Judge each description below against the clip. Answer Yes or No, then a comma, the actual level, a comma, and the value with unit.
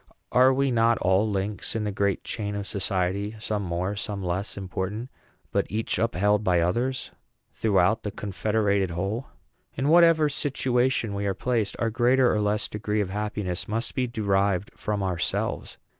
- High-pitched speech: No, low, 105 Hz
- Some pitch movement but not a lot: Yes, average, 3.1 semitones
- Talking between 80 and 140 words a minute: No, average, 160 wpm